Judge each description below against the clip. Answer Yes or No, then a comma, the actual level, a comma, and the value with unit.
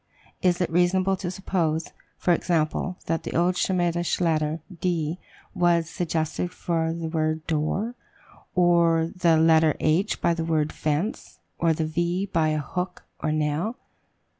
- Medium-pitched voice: Yes, medium, 165 Hz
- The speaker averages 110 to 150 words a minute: Yes, average, 145 wpm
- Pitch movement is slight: Yes, narrow, 2.1 semitones